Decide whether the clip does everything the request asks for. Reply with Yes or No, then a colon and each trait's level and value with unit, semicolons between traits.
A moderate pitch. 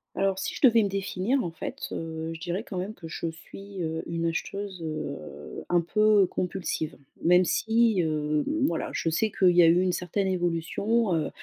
Yes: medium, 180 Hz